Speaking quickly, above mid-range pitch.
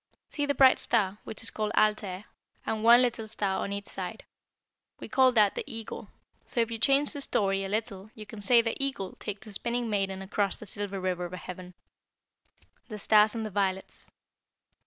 No: average, 195 wpm; high, 215 Hz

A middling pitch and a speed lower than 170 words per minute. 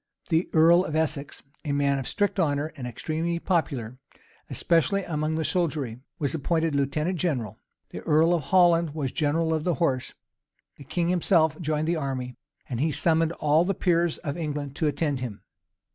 No: medium, 155 Hz; average, 175 wpm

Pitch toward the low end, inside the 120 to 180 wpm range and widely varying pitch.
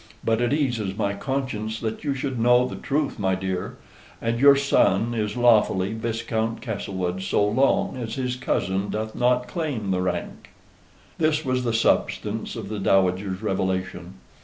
No: low, 110 Hz; average, 160 wpm; average, 4.4 semitones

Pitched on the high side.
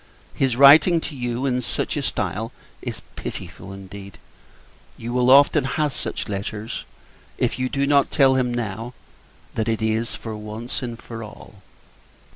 No: low, 120 Hz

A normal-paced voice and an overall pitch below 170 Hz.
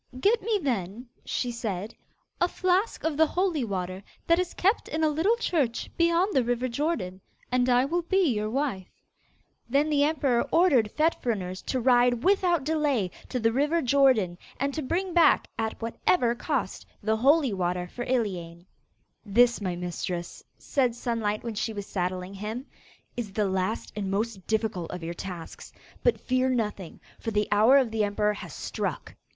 No: average, 170 wpm; high, 240 Hz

